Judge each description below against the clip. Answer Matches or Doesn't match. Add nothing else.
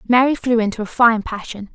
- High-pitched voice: Matches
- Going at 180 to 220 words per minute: Matches